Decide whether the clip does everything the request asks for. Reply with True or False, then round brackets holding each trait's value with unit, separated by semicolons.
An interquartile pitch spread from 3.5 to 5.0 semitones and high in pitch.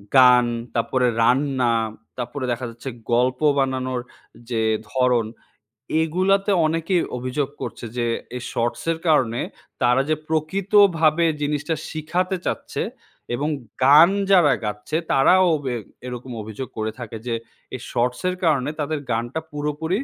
False (4.5 semitones; 135 Hz)